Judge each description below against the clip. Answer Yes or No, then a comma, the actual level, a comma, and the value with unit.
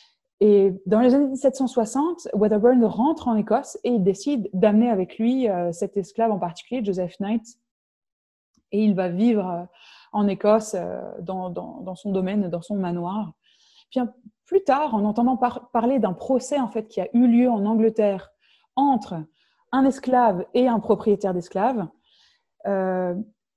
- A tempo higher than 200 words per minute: No, average, 165 wpm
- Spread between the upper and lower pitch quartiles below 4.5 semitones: Yes, average, 4.1 semitones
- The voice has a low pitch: No, high, 220 Hz